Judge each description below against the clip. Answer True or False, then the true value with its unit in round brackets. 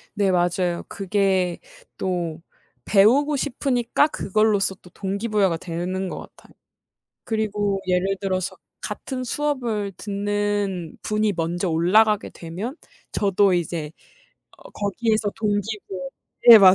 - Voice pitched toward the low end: False (200 Hz)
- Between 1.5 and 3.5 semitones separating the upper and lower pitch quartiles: True (2.9 semitones)